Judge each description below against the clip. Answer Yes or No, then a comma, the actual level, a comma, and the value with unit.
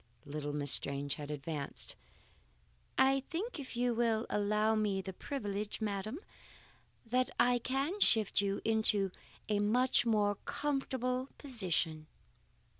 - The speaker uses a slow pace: Yes, slow, 120 wpm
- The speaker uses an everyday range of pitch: Yes, average, 4.7 semitones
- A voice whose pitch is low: No, high, 215 Hz